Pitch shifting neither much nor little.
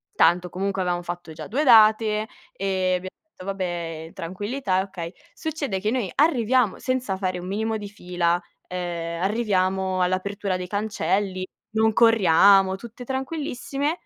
Yes: average, 3.5 semitones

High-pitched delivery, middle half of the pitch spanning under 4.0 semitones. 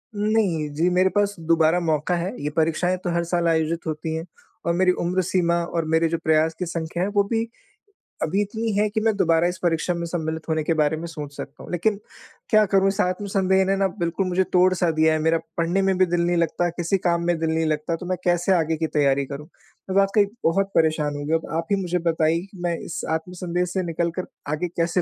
No: medium, 170 Hz; narrow, 2.5 semitones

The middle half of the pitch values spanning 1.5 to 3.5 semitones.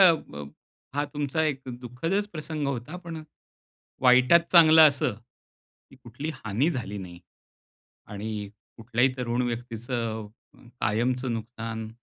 No: average, 4.8 semitones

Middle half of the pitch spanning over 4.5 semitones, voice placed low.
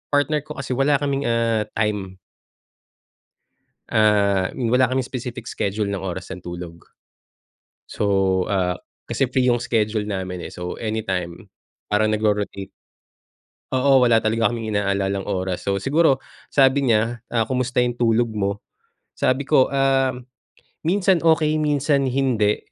Yes: average, 4.9 semitones; low, 115 Hz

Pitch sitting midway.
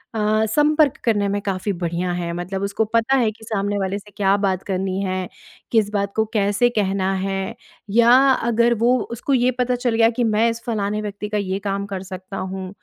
No: high, 205 Hz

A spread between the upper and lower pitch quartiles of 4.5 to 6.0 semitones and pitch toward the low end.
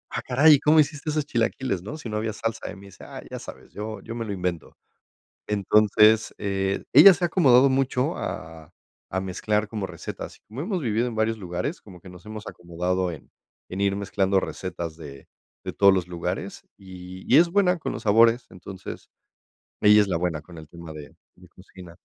Yes: average, 4.8 semitones; low, 100 Hz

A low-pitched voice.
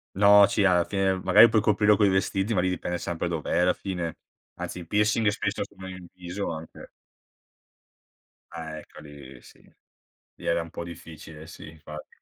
Yes: very low, 90 Hz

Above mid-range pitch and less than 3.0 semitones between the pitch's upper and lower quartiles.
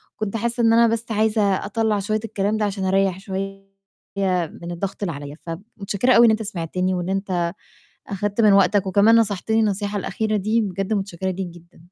Yes: high, 200 Hz; narrow, 2.5 semitones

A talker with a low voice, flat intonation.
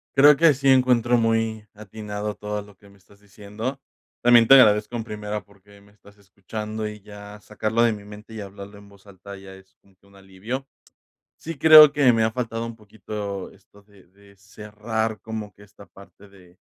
Yes: low, 105 Hz; narrow, 2.0 semitones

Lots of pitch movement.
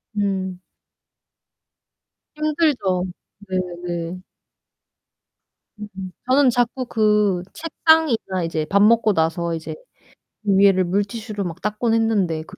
No: average, 4.4 semitones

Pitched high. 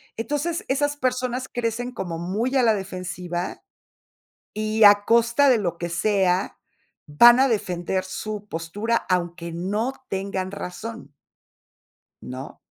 Yes: high, 205 Hz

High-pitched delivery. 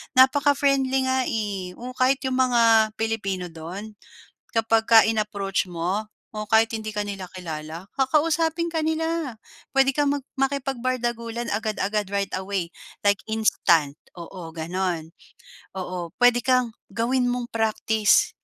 Yes: high, 225 Hz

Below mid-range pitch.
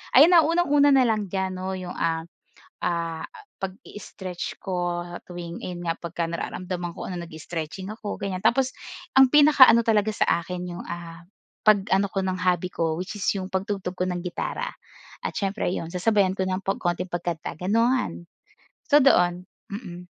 No: medium, 185 Hz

